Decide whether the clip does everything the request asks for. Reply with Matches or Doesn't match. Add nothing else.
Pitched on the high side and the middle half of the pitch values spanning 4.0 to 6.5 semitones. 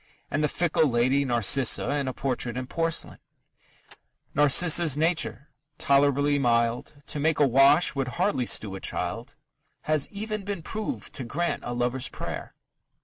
Doesn't match